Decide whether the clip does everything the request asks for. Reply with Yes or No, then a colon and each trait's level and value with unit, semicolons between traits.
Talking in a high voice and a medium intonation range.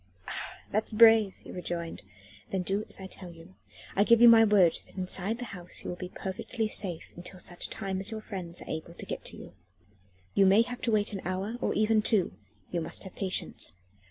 Yes: high, 195 Hz; average, 3.3 semitones